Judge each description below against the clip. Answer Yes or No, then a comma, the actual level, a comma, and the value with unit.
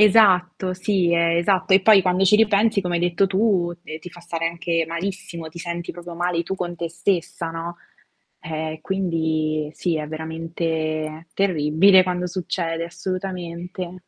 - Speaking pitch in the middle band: Yes, medium, 175 Hz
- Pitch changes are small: Yes, narrow, 2.1 semitones